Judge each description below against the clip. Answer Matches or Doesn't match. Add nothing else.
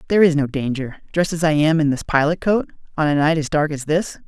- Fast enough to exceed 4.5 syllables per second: Matches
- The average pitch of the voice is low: Doesn't match